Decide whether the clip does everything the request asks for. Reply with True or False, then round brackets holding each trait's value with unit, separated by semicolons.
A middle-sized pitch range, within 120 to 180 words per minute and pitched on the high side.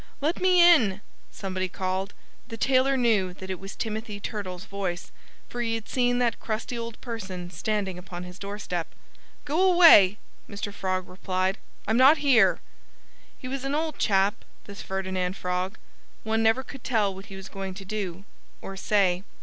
True (4.2 semitones; 165 wpm; 205 Hz)